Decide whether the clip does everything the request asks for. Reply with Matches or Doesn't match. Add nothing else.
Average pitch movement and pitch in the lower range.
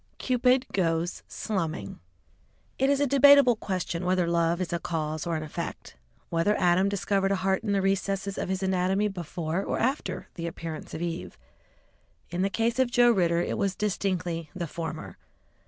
Doesn't match